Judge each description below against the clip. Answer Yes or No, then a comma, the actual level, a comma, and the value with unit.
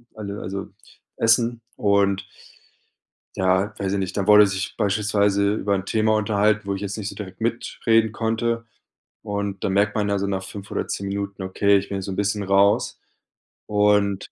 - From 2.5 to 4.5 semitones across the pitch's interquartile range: No, narrow, 1.3 semitones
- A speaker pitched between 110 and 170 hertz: No, low, 100 Hz